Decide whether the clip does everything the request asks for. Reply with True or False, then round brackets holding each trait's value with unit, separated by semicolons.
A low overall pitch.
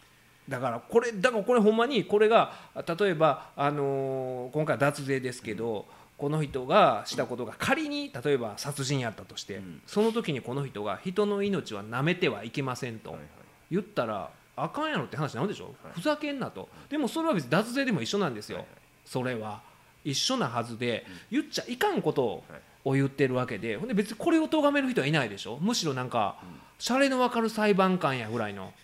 False (155 Hz)